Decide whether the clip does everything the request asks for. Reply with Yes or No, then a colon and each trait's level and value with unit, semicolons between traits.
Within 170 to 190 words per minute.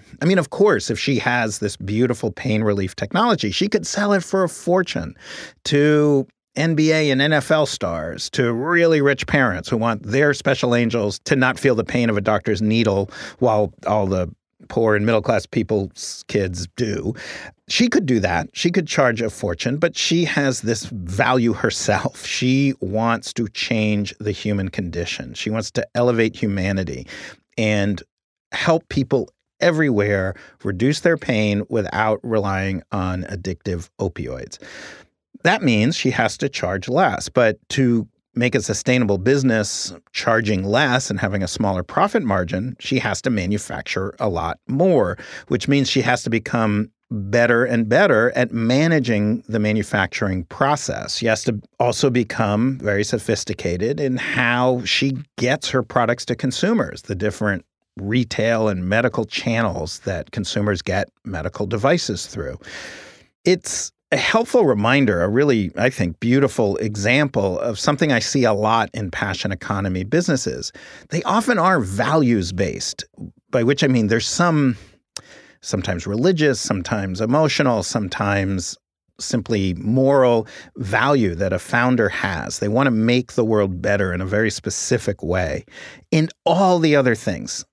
No: average, 150 wpm